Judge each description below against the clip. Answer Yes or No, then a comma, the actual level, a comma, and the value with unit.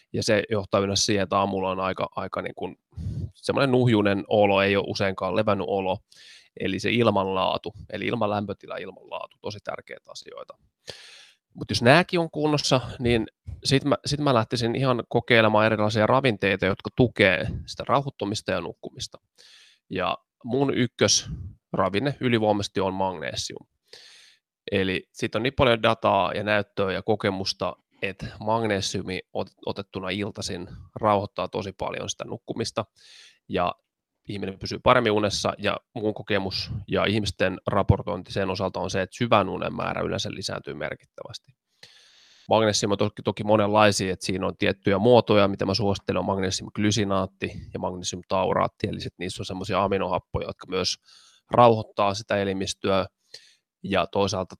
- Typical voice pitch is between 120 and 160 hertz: No, low, 105 Hz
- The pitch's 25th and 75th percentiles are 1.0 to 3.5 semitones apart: Yes, average, 2.8 semitones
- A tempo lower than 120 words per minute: No, average, 140 wpm